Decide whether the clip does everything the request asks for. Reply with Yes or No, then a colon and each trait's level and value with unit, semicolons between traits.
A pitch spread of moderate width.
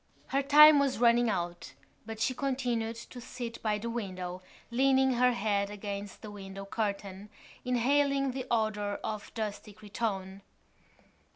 Yes: average, 3.8 semitones